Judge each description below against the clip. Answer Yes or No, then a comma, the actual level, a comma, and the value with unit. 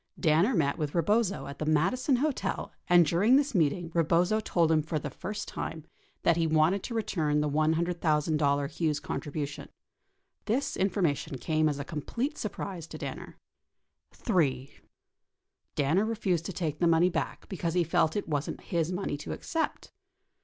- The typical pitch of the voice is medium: Yes, medium, 165 Hz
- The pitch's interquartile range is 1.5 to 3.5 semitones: No, average, 4.1 semitones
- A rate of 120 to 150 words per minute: No, average, 160 wpm